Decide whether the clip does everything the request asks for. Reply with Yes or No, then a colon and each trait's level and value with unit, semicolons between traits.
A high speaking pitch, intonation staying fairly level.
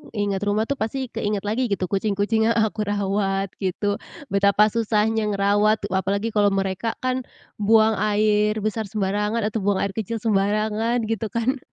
Yes: high, 210 Hz; narrow, 1.8 semitones